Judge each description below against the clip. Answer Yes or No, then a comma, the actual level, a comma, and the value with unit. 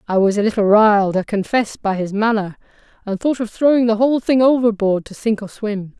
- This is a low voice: No, high, 215 Hz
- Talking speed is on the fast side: Yes, fast, 220 wpm